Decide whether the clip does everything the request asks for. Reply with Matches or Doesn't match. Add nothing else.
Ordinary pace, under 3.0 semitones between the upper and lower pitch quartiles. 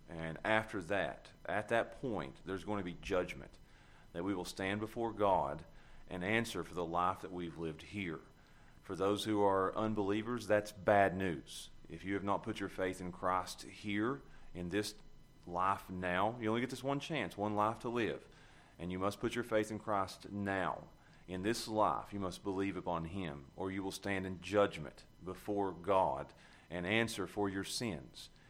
Matches